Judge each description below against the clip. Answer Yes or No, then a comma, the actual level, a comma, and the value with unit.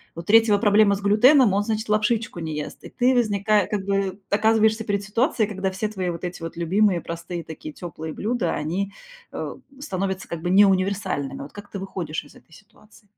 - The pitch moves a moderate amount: Yes, average, 3.3 semitones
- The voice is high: Yes, high, 200 Hz